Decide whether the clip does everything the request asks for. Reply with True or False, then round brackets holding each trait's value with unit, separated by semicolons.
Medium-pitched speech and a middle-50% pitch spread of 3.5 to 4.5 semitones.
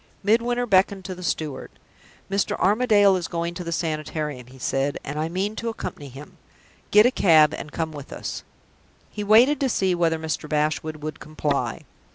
False (170 Hz; 5.0 semitones)